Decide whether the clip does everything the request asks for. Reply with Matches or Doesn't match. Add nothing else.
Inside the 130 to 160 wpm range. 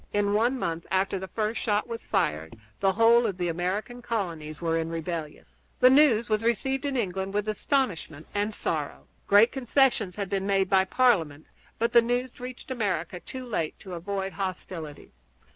Doesn't match